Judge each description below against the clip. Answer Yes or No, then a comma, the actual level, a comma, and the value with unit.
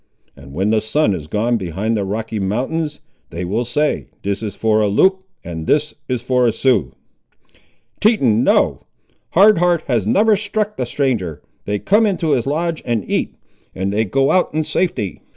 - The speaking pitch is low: Yes, low, 120 Hz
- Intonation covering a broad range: Yes, wide, 7.9 semitones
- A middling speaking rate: Yes, average, 170 wpm